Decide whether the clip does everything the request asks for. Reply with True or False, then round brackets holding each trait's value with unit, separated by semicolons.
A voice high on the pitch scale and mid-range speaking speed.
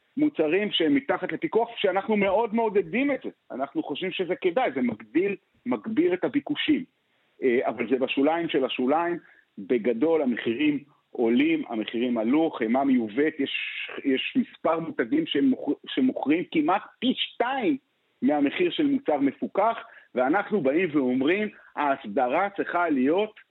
True (210 Hz; 125 wpm)